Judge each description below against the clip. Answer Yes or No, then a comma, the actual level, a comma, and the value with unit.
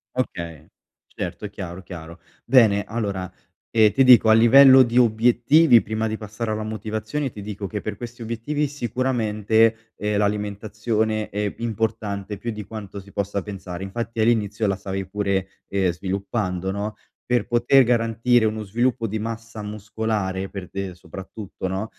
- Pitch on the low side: Yes, low, 110 Hz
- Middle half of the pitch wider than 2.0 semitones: Yes, narrow, 2.6 semitones